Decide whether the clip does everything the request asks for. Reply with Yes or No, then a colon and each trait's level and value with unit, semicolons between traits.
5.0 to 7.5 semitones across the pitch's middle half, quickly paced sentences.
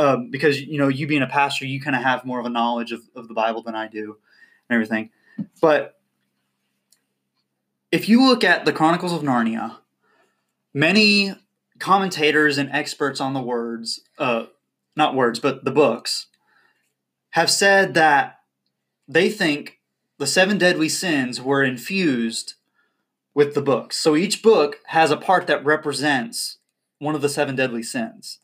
No: wide, 5.4 semitones; average, 160 wpm